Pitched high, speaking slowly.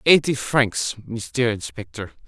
No: low, 115 Hz; slow, 105 wpm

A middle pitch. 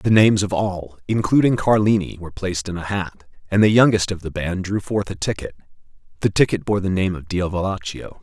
No: very low, 95 Hz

